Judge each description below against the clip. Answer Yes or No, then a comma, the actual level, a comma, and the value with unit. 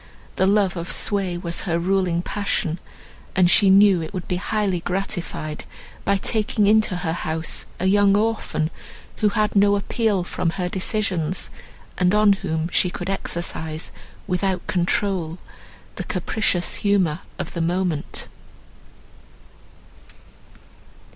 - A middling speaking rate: No, slow, 130 wpm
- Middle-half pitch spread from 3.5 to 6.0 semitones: No, average, 2.7 semitones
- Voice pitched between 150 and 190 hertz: Yes, medium, 185 Hz